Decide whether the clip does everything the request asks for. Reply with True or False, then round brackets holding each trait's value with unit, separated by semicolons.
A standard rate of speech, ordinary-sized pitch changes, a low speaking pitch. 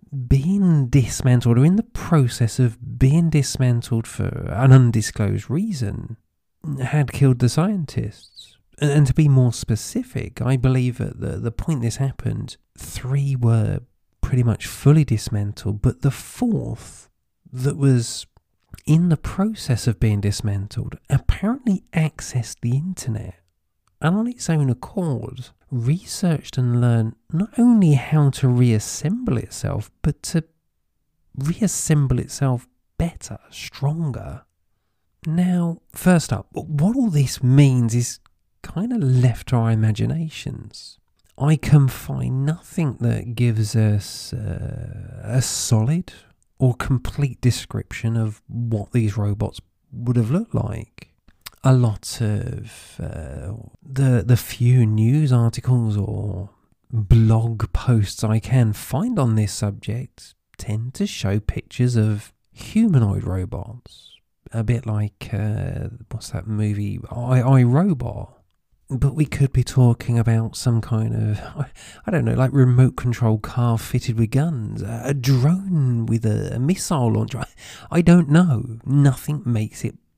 False (130 wpm; 4.1 semitones; 120 Hz)